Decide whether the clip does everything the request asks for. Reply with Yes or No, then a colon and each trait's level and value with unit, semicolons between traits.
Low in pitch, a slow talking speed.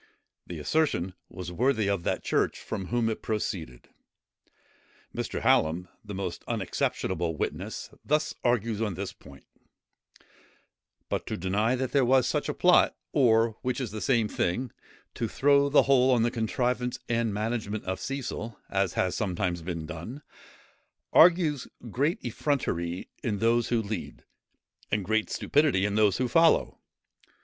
No: low, 110 Hz; average, 145 wpm